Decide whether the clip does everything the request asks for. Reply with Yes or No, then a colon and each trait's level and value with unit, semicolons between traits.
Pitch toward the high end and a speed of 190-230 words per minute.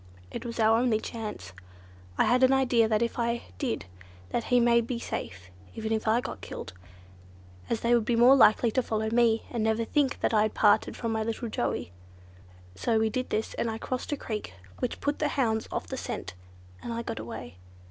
Yes: high, 230 Hz; fast, 205 wpm